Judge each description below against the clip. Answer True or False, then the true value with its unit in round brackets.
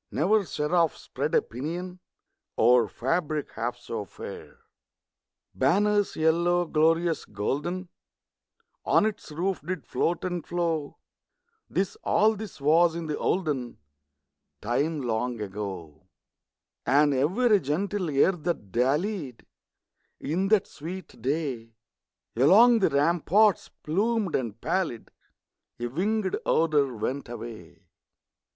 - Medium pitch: True (160 Hz)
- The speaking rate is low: True (110 wpm)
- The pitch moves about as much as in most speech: False (6.3 semitones)